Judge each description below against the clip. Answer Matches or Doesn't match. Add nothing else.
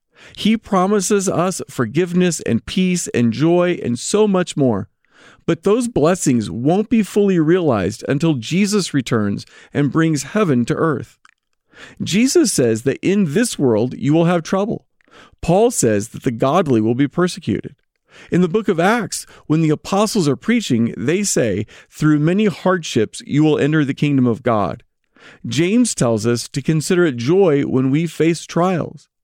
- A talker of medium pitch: Matches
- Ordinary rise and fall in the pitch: Doesn't match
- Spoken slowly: Doesn't match